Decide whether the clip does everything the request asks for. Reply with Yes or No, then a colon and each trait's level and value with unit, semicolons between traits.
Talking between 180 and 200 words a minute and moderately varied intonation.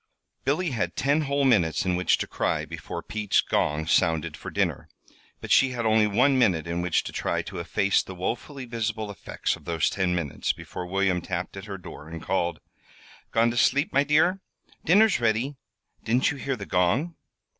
No: average, 190 wpm; wide, 6.9 semitones